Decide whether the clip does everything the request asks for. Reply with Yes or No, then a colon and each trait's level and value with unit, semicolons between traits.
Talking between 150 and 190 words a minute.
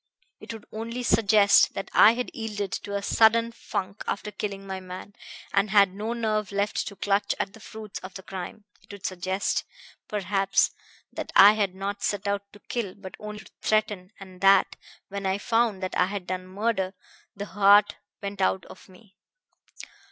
Yes: average, 180 wpm